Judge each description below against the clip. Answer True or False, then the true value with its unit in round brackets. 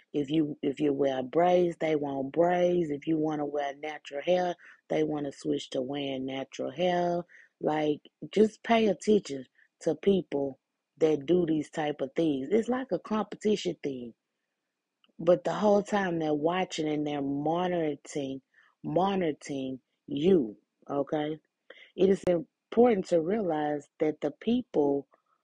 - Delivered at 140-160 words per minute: True (145 wpm)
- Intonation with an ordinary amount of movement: True (3.8 semitones)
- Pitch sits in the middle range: True (155 Hz)